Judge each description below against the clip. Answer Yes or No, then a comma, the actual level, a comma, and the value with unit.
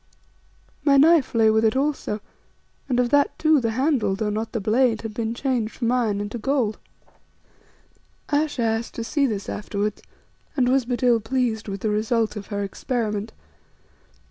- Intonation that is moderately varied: Yes, average, 3.3 semitones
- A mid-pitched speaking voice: No, high, 230 Hz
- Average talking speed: Yes, average, 170 wpm